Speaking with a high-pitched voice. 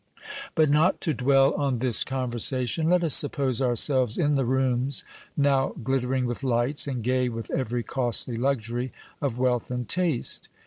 No: low, 130 Hz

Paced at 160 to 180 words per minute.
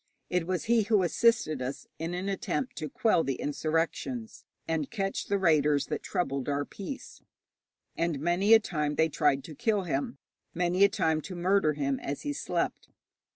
Yes: average, 175 wpm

